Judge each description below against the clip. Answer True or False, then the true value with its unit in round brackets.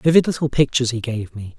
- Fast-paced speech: True (225 wpm)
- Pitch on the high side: False (130 Hz)